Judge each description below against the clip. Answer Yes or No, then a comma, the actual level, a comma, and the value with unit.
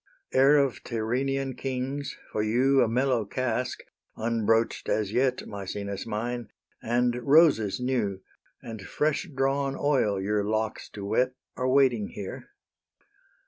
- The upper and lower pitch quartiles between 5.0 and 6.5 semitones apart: No, average, 3.9 semitones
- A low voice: Yes, low, 120 Hz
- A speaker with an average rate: No, slow, 125 wpm